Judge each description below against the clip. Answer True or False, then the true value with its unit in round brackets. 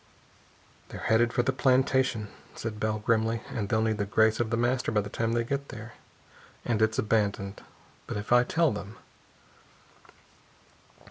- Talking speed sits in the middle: True (160 wpm)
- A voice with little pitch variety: True (2.1 semitones)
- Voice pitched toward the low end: True (110 Hz)